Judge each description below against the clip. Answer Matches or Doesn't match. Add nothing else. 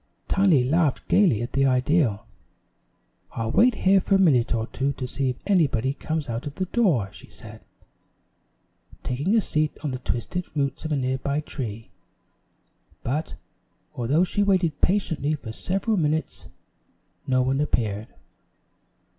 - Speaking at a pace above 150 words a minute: Doesn't match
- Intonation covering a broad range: Matches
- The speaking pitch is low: Doesn't match